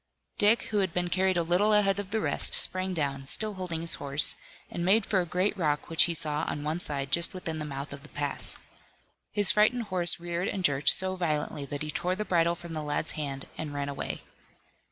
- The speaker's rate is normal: No, fast, 225 wpm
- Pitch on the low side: No, medium, 170 Hz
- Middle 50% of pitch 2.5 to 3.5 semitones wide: No, average, 4.1 semitones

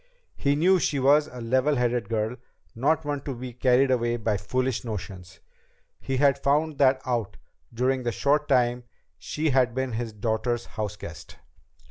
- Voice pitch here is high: No, low, 125 Hz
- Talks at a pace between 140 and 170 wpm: Yes, average, 165 wpm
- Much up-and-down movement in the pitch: No, average, 3.2 semitones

